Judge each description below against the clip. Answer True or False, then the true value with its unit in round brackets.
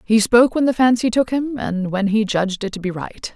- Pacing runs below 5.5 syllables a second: False (5.6 syllables/s)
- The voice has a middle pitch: False (220 Hz)